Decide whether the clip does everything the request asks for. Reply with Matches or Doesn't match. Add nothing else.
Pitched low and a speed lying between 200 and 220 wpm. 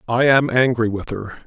Matches